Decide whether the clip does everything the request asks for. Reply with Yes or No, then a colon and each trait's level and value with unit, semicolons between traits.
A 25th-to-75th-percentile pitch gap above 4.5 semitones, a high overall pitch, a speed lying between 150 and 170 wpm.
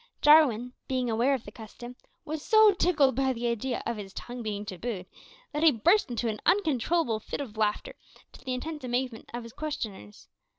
No: average, 4.9 semitones; high, 245 Hz; average, 185 wpm